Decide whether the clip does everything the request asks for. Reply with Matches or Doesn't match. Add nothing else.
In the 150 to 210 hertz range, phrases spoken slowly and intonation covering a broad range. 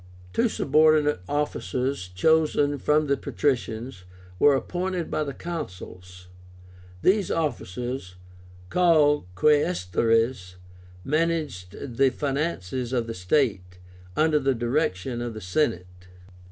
Doesn't match